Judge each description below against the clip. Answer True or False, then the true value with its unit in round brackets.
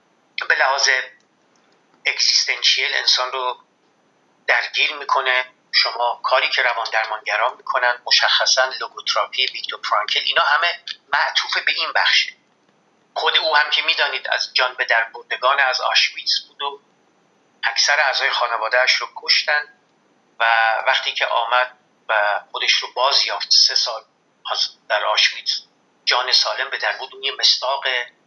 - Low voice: True (125 Hz)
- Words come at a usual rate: True (125 wpm)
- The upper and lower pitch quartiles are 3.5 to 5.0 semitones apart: False (3.0 semitones)